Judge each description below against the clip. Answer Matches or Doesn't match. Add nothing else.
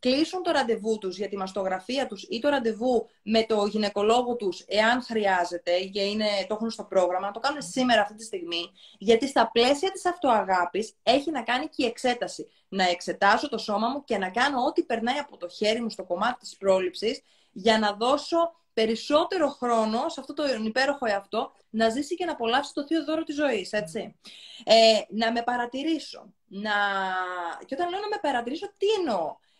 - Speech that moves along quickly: Matches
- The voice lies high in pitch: Matches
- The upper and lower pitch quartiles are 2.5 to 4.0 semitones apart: Doesn't match